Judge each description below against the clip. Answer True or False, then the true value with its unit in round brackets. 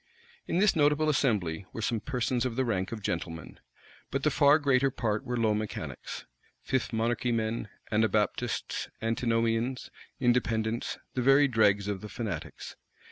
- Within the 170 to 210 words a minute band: False (145 wpm)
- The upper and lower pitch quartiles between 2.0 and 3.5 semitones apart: True (3.2 semitones)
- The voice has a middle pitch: False (115 Hz)